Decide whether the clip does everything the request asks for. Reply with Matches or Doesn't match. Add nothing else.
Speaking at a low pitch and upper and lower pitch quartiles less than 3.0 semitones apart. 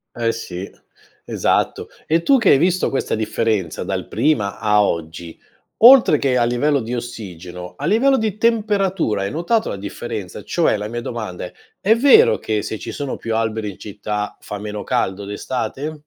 Doesn't match